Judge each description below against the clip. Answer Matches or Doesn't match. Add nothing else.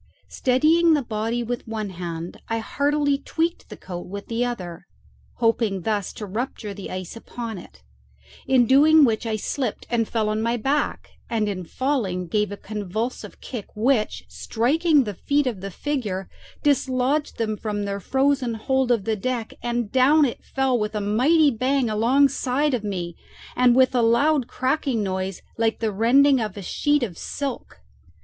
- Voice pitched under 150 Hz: Doesn't match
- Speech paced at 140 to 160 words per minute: Doesn't match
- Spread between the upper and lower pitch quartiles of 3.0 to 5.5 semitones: Matches